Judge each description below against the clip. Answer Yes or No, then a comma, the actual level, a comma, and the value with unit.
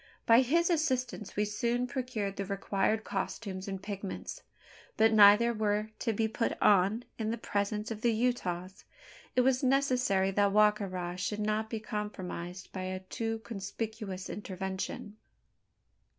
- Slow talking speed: No, average, 150 wpm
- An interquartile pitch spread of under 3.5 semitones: Yes, average, 2.9 semitones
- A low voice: No, high, 210 Hz